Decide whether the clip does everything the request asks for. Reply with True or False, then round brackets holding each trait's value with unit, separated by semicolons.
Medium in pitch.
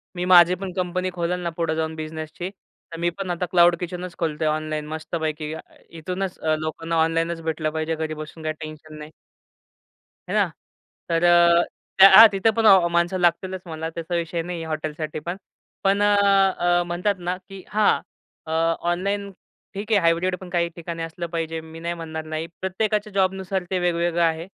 True (170 Hz)